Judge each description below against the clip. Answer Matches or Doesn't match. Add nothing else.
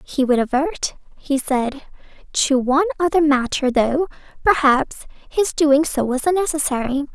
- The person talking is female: Matches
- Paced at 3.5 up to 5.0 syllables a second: Matches